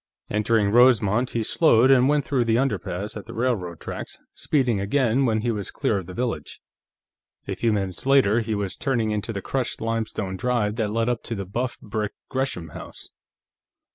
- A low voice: Yes, low, 115 Hz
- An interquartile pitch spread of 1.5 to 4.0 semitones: Yes, average, 3.4 semitones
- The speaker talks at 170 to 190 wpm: Yes, average, 185 wpm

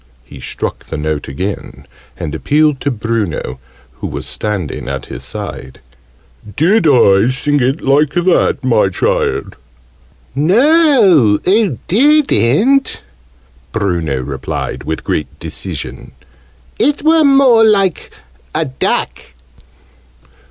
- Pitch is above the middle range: No, low, 135 Hz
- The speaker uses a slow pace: Yes, slow, 110 wpm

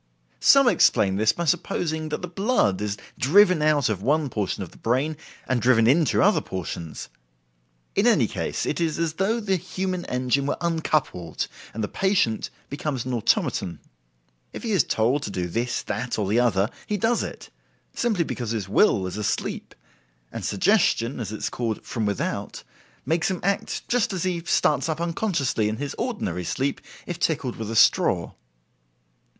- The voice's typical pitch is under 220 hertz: Yes, medium, 140 Hz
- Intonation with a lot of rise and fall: Yes, wide, 8.1 semitones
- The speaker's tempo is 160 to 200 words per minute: Yes, average, 175 wpm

